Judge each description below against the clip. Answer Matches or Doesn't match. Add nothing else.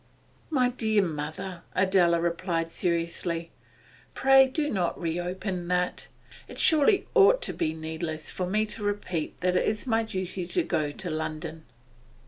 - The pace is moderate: Matches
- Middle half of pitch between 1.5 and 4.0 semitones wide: Doesn't match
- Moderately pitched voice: Matches